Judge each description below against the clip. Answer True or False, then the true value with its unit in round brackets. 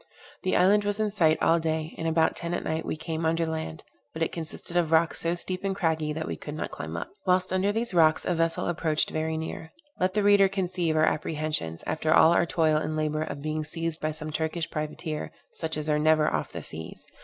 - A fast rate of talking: True (235 wpm)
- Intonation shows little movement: True (1.9 semitones)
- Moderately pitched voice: True (160 Hz)